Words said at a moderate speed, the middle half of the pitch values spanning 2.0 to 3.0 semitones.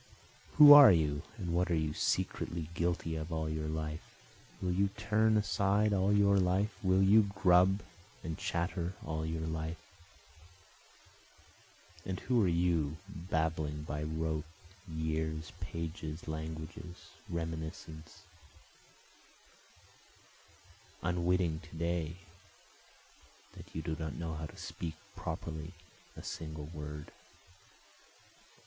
No: slow, 115 wpm; average, 2.7 semitones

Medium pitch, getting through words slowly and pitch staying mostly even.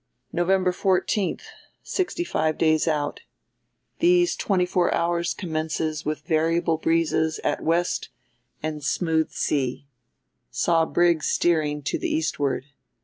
Yes: medium, 165 Hz; slow, 110 wpm; narrow, 2.1 semitones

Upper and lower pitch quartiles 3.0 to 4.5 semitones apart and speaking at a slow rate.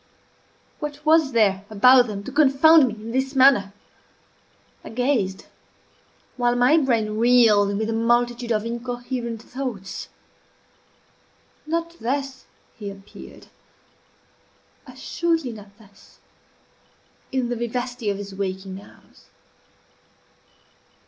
Yes: average, 4.0 semitones; slow, 105 wpm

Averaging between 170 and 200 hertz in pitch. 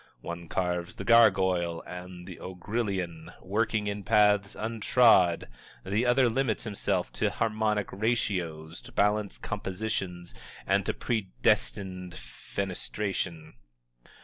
No: low, 100 Hz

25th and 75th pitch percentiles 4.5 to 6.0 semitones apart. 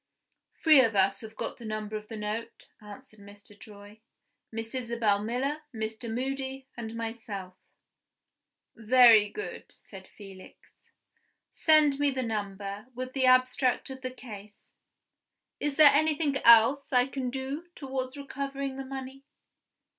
No: average, 4.0 semitones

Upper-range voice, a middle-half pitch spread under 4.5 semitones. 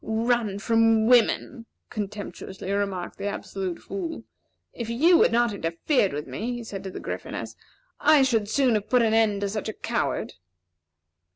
Yes: high, 220 Hz; average, 3.1 semitones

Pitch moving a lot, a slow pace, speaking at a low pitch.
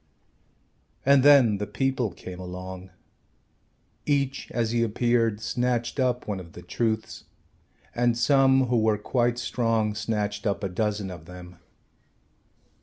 No: average, 3.4 semitones; slow, 130 wpm; low, 110 Hz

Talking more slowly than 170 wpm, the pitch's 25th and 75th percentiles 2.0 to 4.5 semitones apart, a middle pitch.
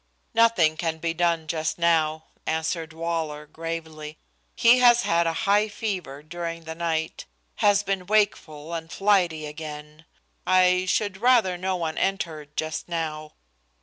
Yes: slow, 135 wpm; average, 3.0 semitones; medium, 165 Hz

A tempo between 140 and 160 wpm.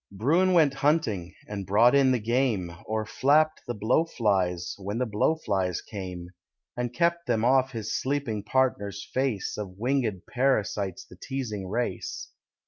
Yes: average, 150 wpm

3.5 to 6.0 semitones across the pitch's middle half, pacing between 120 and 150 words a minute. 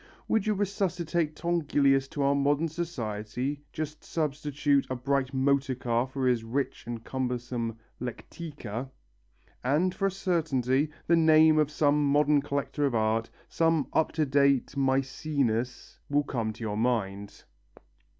Yes: average, 3.8 semitones; average, 140 wpm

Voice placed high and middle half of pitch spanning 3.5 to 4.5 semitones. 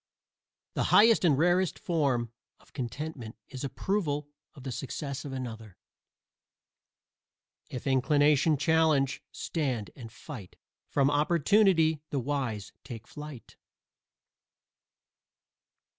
No: medium, 140 Hz; average, 4.0 semitones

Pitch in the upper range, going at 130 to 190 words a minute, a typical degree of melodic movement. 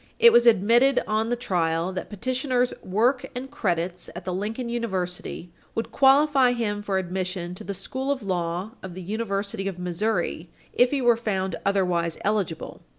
Yes: high, 205 Hz; average, 165 wpm; average, 4.9 semitones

